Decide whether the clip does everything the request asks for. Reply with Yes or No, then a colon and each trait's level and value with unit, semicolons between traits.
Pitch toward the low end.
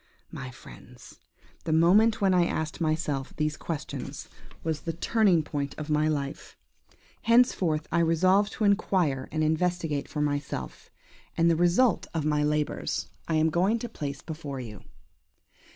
No: medium, 160 Hz